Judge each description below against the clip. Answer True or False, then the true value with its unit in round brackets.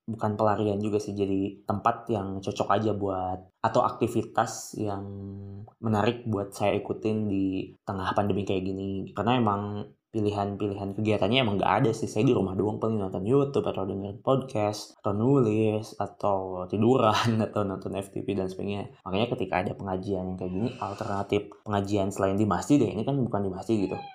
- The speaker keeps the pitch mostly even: True (1.9 semitones)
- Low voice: True (100 Hz)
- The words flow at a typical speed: False (170 wpm)